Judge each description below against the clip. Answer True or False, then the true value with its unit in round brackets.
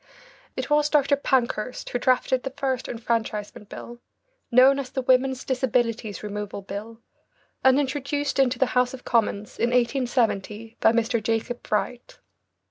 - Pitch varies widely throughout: False (2.8 semitones)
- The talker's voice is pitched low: False (245 Hz)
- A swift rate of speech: False (140 wpm)